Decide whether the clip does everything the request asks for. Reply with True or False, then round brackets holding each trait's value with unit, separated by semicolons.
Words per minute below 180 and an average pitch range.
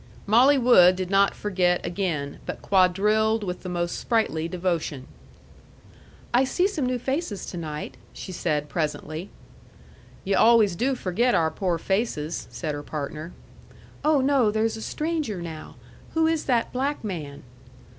False (145 wpm; 6.3 semitones)